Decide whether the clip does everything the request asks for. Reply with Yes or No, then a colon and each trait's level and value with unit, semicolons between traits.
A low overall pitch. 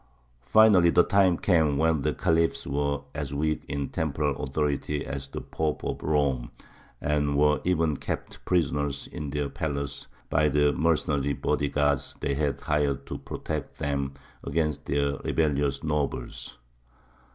Yes: very low, 75 Hz